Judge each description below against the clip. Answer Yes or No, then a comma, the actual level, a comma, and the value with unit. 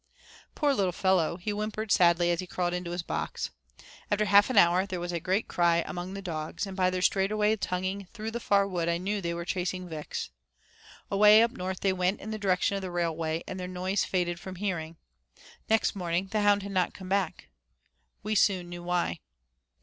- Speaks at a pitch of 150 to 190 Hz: Yes, medium, 185 Hz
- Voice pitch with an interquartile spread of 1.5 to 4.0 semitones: Yes, narrow, 2.4 semitones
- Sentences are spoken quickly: Yes, fast, 210 wpm